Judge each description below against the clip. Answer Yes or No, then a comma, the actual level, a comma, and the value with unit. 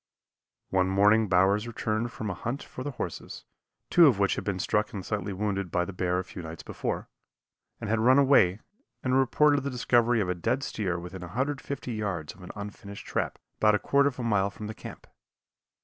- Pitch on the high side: No, low, 105 Hz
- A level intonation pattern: No, average, 4.5 semitones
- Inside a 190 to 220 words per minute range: Yes, average, 200 wpm